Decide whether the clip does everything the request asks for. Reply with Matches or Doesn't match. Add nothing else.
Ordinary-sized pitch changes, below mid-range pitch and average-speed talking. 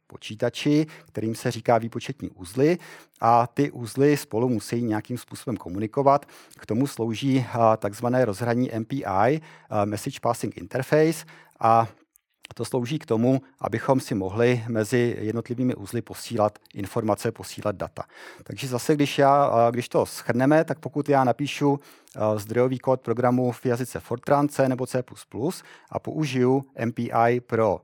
Matches